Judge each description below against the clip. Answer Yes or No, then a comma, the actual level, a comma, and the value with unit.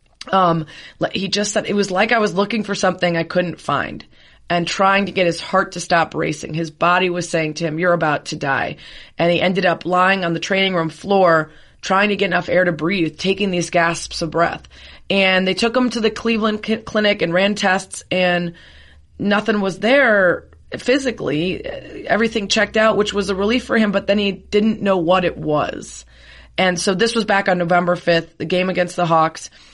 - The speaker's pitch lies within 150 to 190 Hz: Yes, medium, 185 Hz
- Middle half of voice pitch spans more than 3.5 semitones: No, average, 3.2 semitones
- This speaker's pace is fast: Yes, fast, 210 wpm